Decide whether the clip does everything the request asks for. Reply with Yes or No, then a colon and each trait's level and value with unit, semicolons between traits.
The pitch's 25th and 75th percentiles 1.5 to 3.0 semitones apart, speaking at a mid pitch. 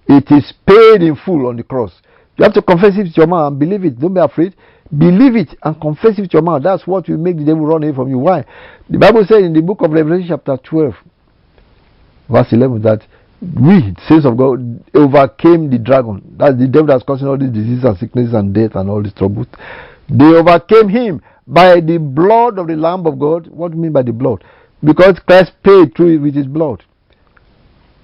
No: average, 4.8 semitones; medium, 155 Hz